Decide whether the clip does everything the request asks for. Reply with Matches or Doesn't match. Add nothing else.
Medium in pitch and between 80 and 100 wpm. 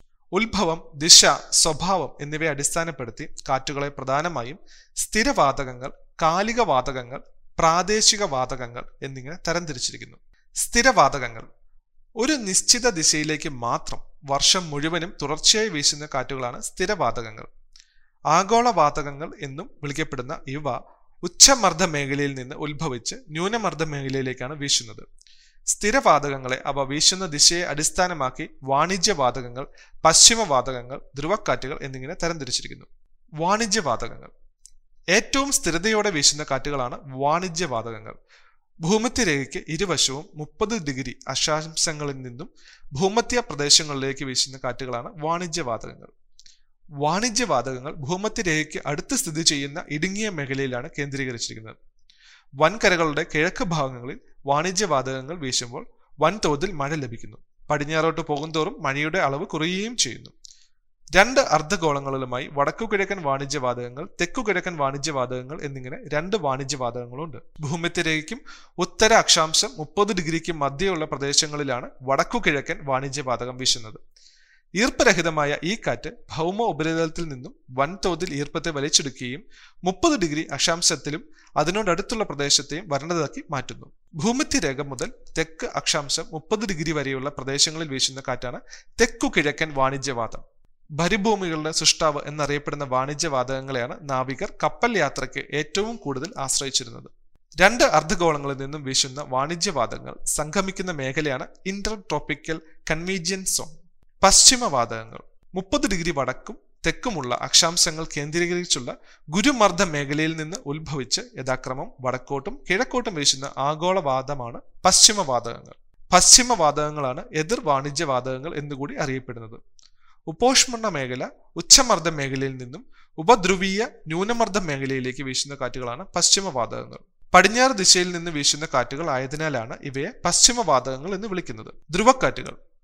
Matches